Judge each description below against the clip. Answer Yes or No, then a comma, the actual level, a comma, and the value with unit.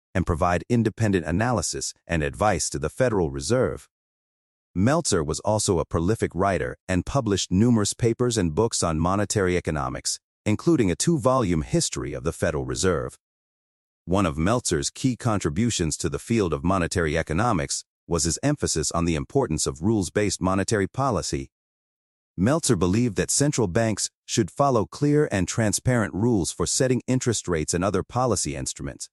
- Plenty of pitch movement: Yes, wide, 6.0 semitones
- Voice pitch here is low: Yes, very low, 95 Hz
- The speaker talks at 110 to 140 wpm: No, average, 155 wpm